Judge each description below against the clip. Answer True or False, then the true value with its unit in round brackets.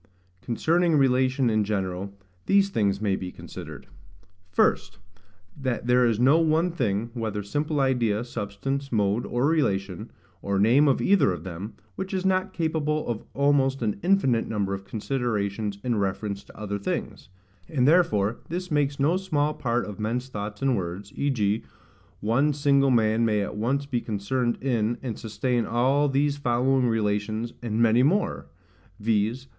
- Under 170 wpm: True (155 wpm)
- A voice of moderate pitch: False (120 Hz)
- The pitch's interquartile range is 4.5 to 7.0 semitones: True (5.1 semitones)